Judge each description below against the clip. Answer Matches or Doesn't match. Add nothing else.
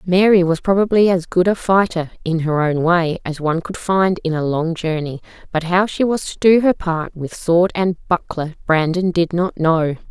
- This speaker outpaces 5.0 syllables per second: Doesn't match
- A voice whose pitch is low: Doesn't match